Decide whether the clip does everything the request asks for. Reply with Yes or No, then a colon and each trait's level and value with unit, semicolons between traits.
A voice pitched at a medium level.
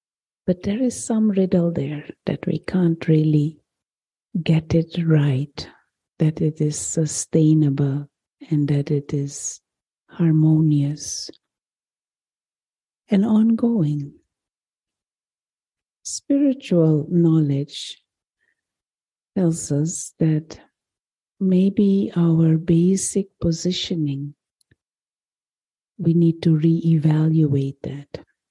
Yes: medium, 160 Hz